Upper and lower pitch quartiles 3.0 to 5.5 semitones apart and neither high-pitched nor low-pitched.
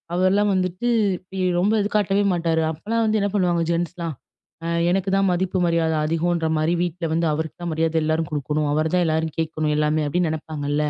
No: narrow, 2.6 semitones; medium, 165 Hz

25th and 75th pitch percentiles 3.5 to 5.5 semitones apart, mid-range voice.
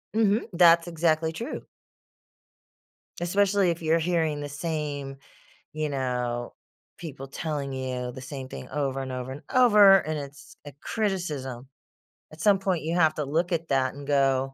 Yes: average, 4.2 semitones; medium, 150 Hz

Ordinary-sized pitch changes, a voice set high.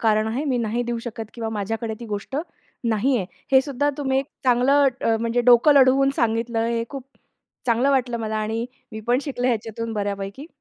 Yes: average, 3.0 semitones; high, 235 Hz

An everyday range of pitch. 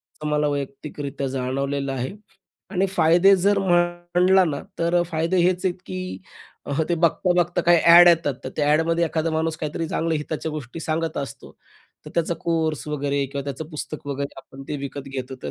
Yes: average, 3.5 semitones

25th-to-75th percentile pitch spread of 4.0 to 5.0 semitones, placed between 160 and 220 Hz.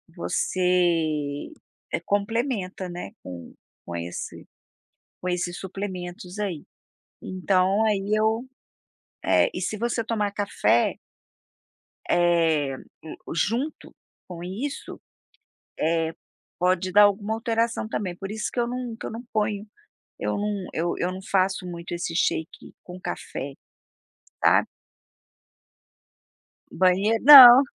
No: average, 3.6 semitones; high, 190 Hz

